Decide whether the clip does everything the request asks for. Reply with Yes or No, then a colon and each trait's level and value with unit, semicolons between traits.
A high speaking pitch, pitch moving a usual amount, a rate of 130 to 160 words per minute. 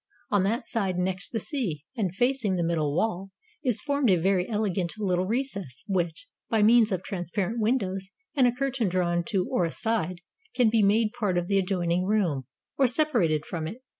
No: high, 195 Hz; average, 4.4 semitones; average, 185 wpm